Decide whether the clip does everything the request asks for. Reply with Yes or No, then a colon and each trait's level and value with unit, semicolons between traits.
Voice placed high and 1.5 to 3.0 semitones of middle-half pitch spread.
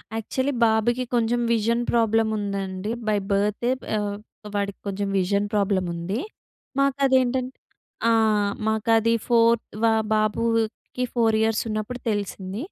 Yes: high, 220 Hz; narrow, 2.4 semitones